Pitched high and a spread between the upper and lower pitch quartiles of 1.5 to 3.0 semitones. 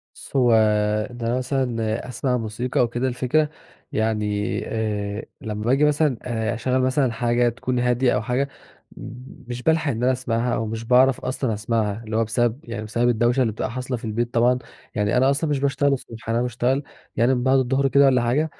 No: low, 120 Hz; narrow, 2.4 semitones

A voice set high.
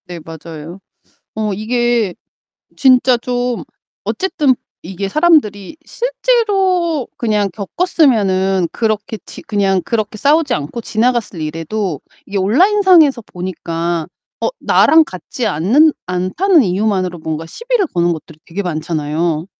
Yes: high, 210 Hz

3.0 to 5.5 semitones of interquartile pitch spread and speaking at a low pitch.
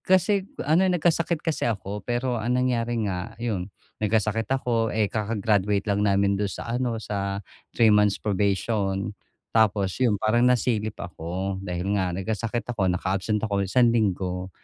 Yes: average, 3.3 semitones; low, 105 Hz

